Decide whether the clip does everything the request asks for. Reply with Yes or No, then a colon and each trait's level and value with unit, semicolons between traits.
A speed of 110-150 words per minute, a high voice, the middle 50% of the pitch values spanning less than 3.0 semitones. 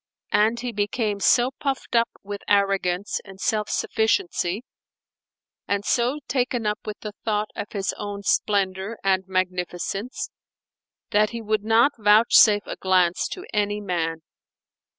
Yes: slow, 135 wpm; high, 210 Hz; narrow, 2.6 semitones